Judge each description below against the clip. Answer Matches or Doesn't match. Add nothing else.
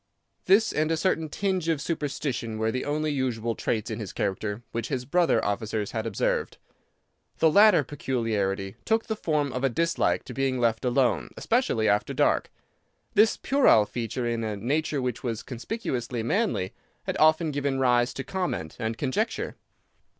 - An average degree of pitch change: Doesn't match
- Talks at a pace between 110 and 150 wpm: Doesn't match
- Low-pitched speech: Matches